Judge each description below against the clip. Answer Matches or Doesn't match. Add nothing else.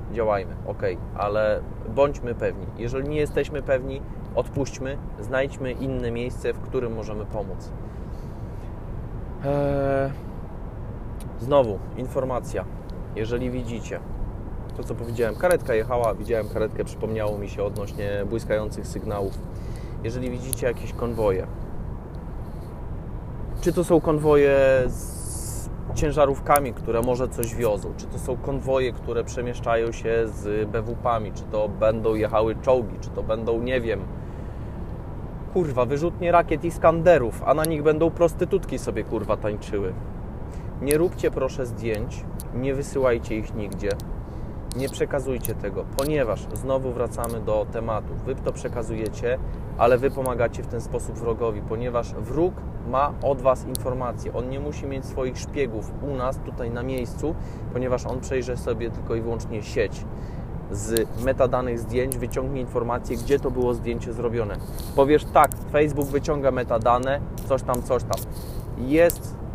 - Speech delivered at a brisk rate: Doesn't match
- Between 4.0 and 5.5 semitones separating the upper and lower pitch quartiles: Doesn't match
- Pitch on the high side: Doesn't match